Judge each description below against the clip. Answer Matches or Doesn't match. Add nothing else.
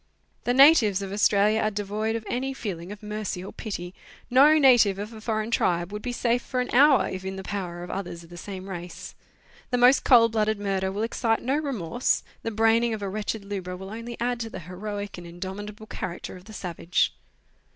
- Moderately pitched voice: Doesn't match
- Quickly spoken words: Matches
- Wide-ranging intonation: Doesn't match